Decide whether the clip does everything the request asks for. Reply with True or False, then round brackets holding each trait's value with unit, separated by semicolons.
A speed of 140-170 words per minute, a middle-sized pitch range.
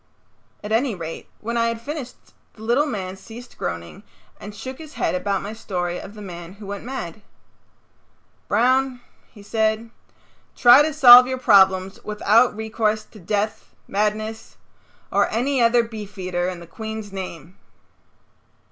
True (145 wpm; 3.6 semitones)